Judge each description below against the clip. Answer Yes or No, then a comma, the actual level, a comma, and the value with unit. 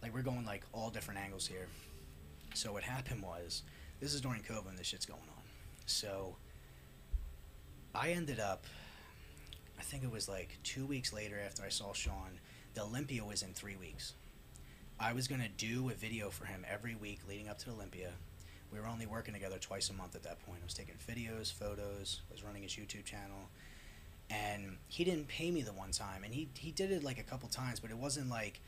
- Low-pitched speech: Yes, low, 100 Hz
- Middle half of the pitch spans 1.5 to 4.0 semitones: No, average, 4.8 semitones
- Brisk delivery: Yes, fast, 210 wpm